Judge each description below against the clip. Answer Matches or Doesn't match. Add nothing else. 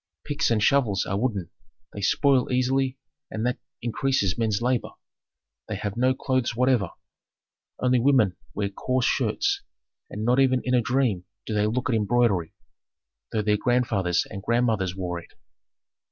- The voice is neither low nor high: Doesn't match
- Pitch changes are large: Doesn't match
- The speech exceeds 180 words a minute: Doesn't match